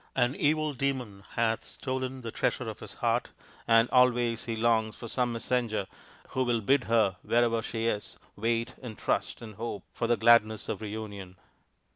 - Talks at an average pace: Yes, average, 170 wpm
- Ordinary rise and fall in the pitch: No, narrow, 2.1 semitones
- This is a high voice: No, low, 115 Hz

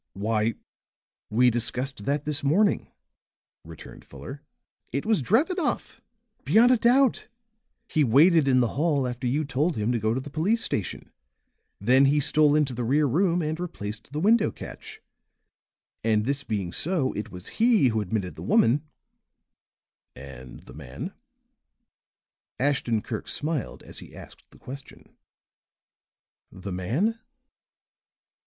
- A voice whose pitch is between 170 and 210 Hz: No, low, 135 Hz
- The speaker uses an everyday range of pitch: No, wide, 6.3 semitones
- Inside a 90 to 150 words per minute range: Yes, average, 140 wpm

